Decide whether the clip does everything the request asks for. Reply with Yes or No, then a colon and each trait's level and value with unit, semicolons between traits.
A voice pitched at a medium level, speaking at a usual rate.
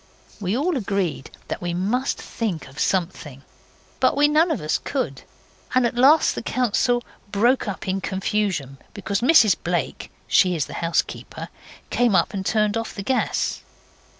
No: high, 200 Hz; average, 160 wpm